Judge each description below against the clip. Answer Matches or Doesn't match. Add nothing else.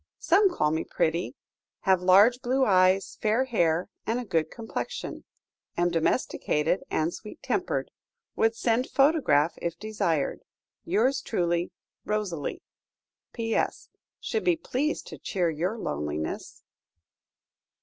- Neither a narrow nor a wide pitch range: Doesn't match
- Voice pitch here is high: Matches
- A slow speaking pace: Matches